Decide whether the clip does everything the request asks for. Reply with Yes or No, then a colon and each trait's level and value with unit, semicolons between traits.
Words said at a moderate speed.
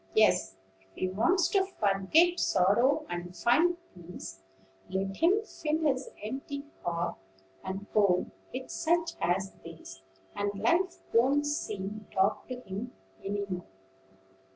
No: slow, 130 wpm